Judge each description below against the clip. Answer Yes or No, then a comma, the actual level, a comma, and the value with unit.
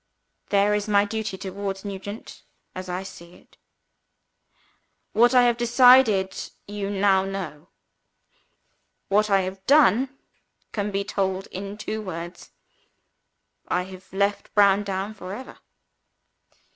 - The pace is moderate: No, slow, 120 wpm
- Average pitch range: No, narrow, 1.8 semitones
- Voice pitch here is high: Yes, high, 200 Hz